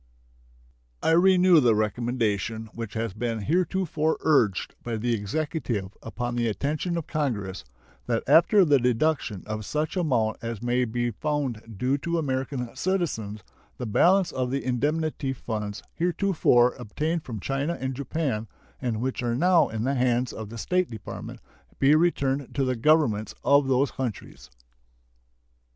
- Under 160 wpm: Yes, average, 145 wpm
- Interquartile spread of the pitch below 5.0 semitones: No, average, 5.3 semitones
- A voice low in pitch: Yes, low, 125 Hz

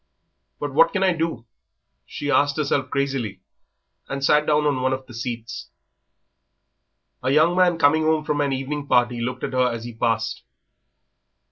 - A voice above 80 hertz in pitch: Yes, medium, 140 Hz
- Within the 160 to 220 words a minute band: Yes, average, 165 wpm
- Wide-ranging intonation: No, average, 3.3 semitones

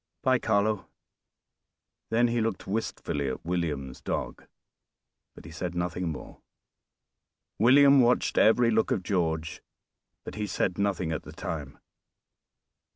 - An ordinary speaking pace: No, slow, 125 wpm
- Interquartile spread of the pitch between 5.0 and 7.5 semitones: Yes, average, 5.3 semitones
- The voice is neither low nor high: No, very low, 95 Hz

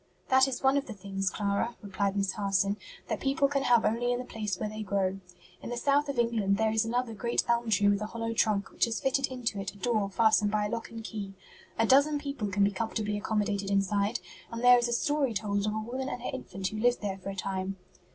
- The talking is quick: Yes, fast, 250 wpm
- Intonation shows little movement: No, average, 3.3 semitones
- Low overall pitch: No, high, 220 Hz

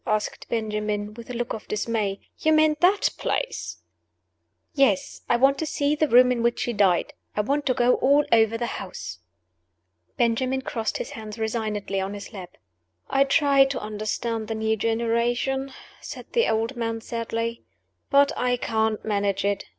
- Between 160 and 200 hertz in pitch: No, high, 230 Hz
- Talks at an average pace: Yes, average, 165 wpm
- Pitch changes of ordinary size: Yes, average, 3.8 semitones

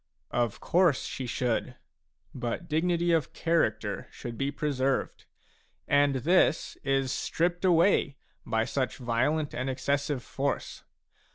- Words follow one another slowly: Yes, slow, 125 wpm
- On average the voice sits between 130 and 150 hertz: Yes, medium, 140 Hz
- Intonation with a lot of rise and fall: No, average, 4.4 semitones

